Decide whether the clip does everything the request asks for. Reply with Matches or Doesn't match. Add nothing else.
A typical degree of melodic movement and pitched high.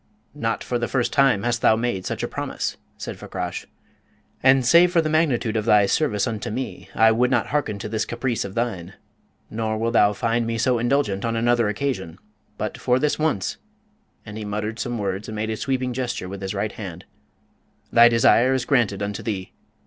Doesn't match